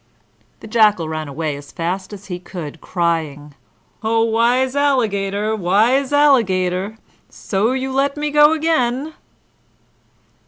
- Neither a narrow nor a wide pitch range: No, wide, 6.7 semitones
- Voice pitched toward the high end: Yes, high, 215 Hz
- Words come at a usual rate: No, slow, 120 wpm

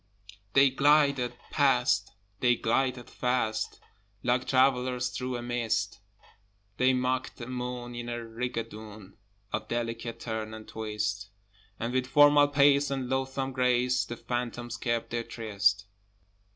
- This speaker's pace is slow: Yes, slow, 125 wpm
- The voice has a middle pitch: No, low, 125 Hz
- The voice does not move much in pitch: Yes, narrow, 2.1 semitones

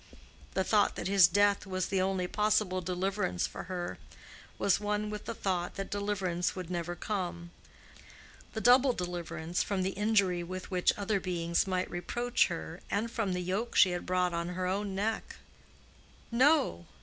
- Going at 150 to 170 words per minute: Yes, average, 160 wpm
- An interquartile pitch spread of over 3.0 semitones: No, narrow, 2.6 semitones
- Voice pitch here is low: No, medium, 185 Hz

